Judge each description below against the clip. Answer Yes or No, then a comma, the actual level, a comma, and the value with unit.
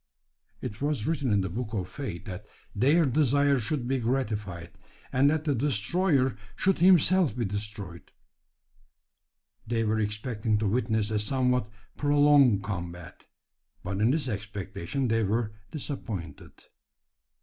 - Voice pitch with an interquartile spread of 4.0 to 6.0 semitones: Yes, average, 5.3 semitones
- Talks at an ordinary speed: No, slow, 130 wpm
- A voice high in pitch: No, low, 115 Hz